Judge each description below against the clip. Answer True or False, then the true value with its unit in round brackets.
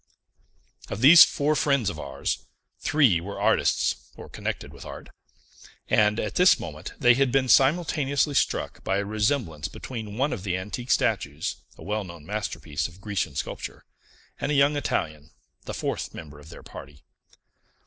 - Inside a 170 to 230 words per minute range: False (160 wpm)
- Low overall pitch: True (105 Hz)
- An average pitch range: False (9.0 semitones)